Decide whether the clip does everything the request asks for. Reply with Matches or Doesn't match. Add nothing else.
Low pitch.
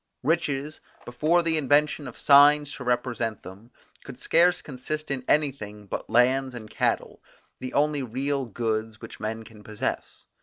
Matches